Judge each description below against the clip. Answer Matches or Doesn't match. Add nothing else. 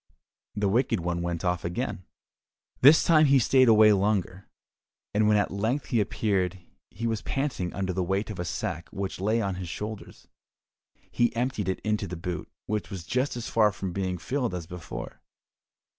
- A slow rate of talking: Doesn't match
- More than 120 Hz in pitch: Doesn't match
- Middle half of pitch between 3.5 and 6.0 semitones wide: Matches